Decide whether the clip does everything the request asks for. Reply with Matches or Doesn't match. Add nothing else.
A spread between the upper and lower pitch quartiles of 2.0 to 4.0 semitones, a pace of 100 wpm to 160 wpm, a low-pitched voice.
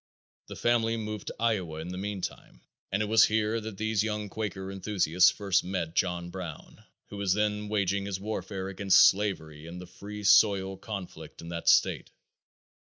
Doesn't match